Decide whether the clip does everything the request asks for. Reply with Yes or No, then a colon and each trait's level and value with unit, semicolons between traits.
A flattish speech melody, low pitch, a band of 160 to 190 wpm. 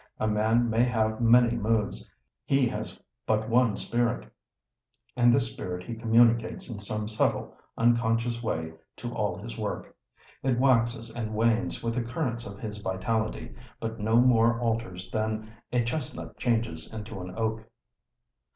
No: narrow, 1.6 semitones; low, 115 Hz; average, 150 wpm